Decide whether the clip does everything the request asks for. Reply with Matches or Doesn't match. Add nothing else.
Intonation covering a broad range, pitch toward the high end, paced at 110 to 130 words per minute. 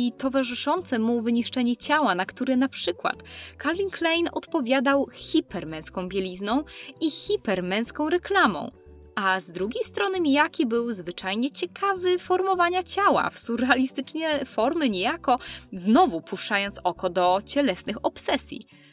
Matches